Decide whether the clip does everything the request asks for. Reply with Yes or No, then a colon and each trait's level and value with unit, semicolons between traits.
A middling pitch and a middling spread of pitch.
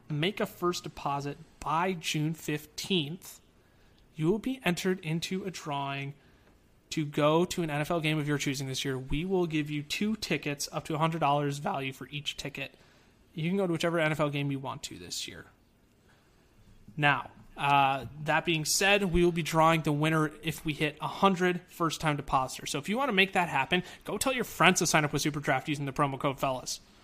Yes: medium, 155 Hz; average, 3.7 semitones